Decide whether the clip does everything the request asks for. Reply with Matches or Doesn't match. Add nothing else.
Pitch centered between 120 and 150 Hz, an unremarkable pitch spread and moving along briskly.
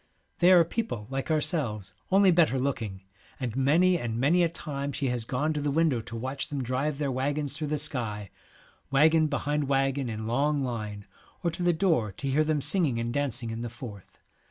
Matches